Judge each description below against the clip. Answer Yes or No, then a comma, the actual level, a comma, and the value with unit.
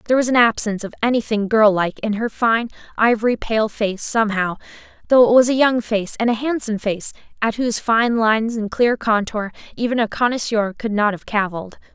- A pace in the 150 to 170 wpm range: No, average, 195 wpm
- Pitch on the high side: Yes, high, 220 Hz